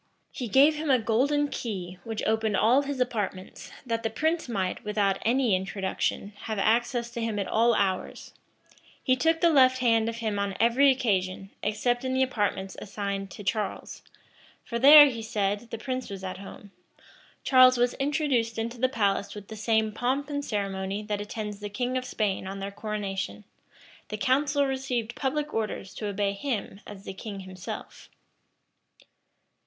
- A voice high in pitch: Yes, high, 225 Hz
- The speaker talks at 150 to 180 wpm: Yes, average, 170 wpm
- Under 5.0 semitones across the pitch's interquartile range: Yes, average, 4.2 semitones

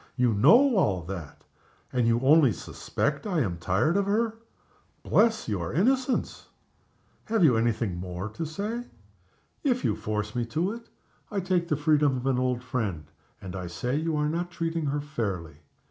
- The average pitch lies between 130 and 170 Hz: Yes, medium, 140 Hz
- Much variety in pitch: Yes, wide, 8.8 semitones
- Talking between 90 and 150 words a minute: No, average, 175 wpm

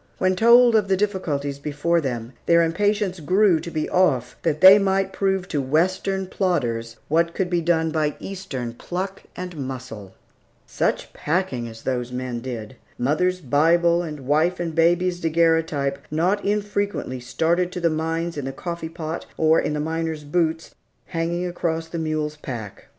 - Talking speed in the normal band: Yes, average, 160 wpm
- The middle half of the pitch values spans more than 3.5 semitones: Yes, average, 4.1 semitones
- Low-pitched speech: No, medium, 165 Hz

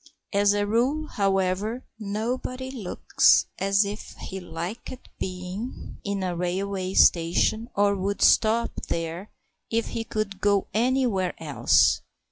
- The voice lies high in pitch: Yes, high, 200 Hz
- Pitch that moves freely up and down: No, average, 3.3 semitones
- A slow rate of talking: Yes, slow, 120 wpm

